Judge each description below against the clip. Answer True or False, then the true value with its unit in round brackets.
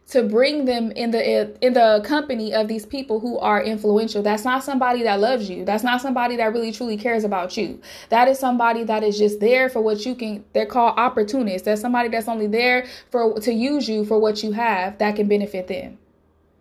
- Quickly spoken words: True (215 wpm)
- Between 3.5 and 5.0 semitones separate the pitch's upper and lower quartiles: False (2.7 semitones)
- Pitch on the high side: True (225 Hz)